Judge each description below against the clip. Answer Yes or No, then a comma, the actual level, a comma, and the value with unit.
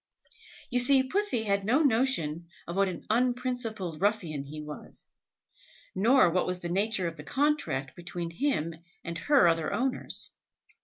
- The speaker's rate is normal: Yes, average, 155 wpm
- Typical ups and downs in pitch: No, wide, 7.0 semitones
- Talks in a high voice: Yes, high, 200 Hz